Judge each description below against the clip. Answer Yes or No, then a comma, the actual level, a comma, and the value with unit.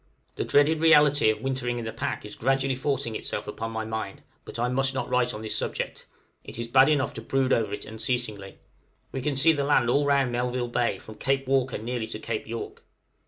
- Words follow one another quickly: Yes, fast, 215 wpm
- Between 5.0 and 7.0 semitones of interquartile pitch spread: No, average, 3.2 semitones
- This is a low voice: Yes, low, 125 Hz